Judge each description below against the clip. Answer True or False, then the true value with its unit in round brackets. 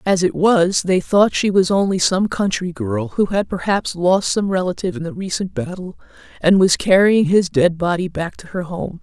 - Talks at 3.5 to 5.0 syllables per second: True (4.8 syllables/s)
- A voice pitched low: False (185 Hz)